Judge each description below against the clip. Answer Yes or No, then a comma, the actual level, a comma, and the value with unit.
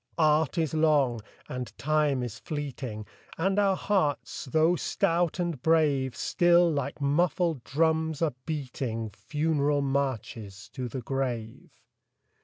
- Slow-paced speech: Yes, slow, 120 wpm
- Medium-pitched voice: Yes, medium, 145 Hz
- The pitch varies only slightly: No, average, 4.0 semitones